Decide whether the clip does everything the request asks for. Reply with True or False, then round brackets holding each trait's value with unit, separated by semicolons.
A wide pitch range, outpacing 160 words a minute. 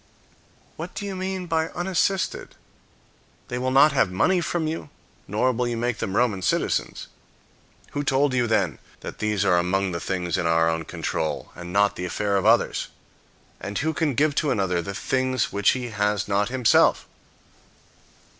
True (6.8 semitones; 175 wpm)